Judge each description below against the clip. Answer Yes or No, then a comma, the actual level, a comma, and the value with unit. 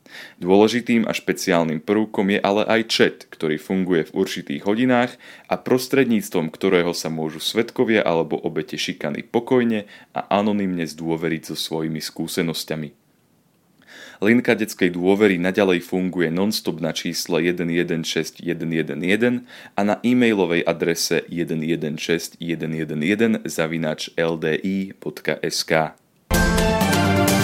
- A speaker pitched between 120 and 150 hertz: No, very low, 90 Hz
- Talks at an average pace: No, slow, 95 wpm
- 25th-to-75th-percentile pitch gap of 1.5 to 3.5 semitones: No, average, 4.6 semitones